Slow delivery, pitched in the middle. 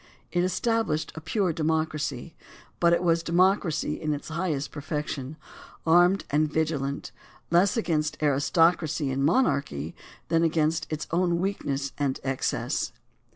Yes: slow, 125 wpm; medium, 160 Hz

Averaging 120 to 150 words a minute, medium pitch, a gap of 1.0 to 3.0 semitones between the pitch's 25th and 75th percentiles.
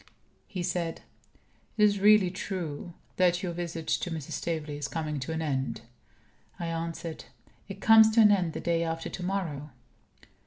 No: average, 165 wpm; medium, 170 Hz; average, 2.7 semitones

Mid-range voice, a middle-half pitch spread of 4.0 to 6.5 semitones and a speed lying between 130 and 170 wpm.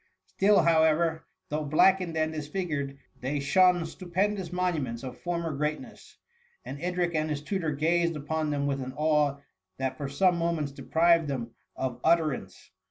No: medium, 155 Hz; average, 3.3 semitones; average, 160 wpm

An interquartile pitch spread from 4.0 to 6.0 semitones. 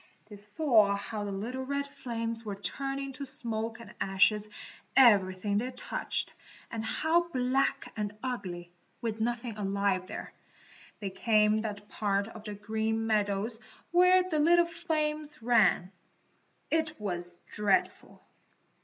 Yes: average, 4.8 semitones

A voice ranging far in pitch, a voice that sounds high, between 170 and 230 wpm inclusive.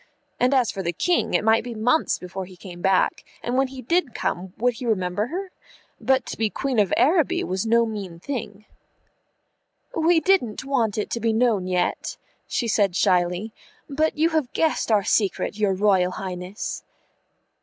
Yes: wide, 5.7 semitones; high, 220 Hz; average, 175 wpm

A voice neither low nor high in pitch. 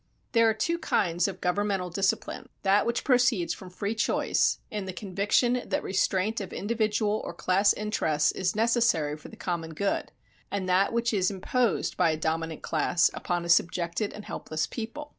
No: high, 195 Hz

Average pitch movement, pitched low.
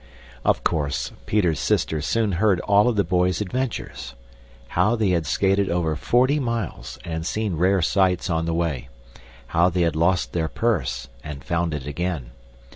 Yes: average, 4.1 semitones; very low, 85 Hz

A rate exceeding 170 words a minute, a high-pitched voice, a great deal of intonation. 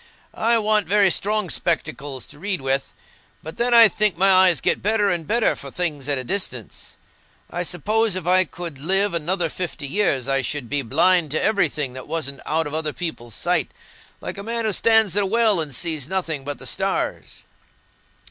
No: average, 195 wpm; medium, 175 Hz; wide, 5.8 semitones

